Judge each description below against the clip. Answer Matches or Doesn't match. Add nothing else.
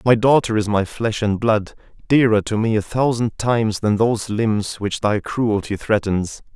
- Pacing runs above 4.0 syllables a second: Matches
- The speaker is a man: Matches